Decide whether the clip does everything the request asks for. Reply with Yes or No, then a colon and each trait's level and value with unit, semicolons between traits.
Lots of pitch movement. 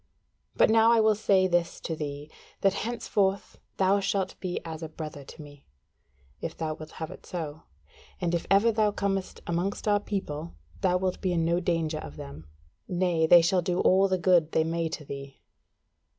No: average, 3.5 semitones